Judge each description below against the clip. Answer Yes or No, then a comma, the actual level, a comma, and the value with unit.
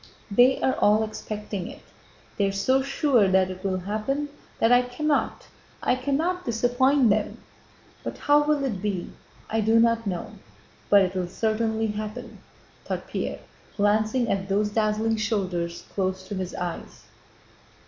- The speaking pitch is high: Yes, high, 215 Hz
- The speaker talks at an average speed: Yes, average, 150 wpm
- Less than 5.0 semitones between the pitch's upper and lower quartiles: Yes, average, 3.9 semitones